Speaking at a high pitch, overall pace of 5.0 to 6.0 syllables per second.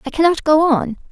Yes: very high, 300 Hz; 5.6 syllables/s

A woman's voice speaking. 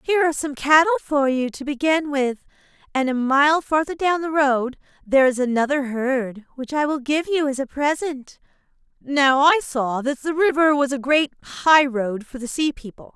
Yes: female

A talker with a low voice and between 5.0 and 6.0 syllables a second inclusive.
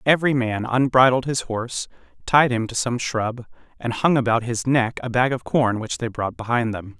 Yes: low, 120 Hz; 5.1 syllables/s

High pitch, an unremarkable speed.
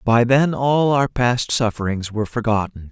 No: low, 120 Hz; average, 165 wpm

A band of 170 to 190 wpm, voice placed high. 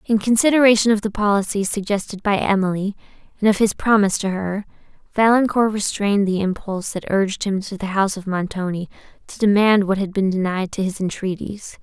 Yes: average, 180 wpm; high, 200 Hz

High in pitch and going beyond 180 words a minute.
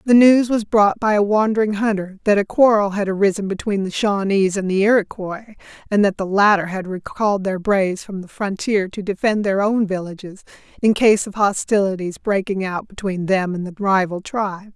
Yes: high, 200 Hz; average, 190 wpm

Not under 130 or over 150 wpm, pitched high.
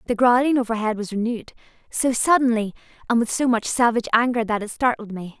No: average, 190 wpm; high, 230 Hz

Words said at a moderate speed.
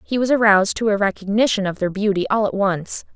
No: fast, 230 wpm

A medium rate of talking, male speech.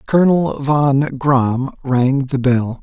No: slow, 130 wpm; male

